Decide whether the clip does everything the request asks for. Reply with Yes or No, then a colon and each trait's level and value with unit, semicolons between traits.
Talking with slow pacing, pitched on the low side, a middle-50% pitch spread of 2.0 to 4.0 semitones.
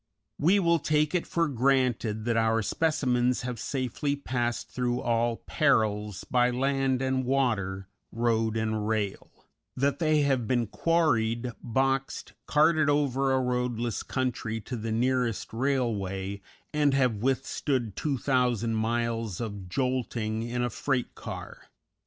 Yes: slow, 130 wpm; low, 125 Hz; average, 3.2 semitones